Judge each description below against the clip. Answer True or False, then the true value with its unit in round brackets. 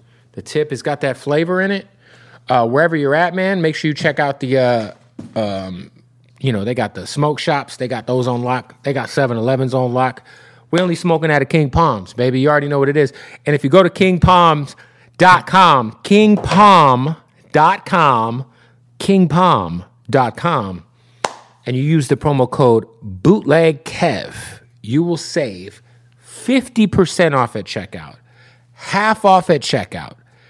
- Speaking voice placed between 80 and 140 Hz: True (135 Hz)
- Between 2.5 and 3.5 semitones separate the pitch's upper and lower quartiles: False (5.2 semitones)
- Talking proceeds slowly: False (155 wpm)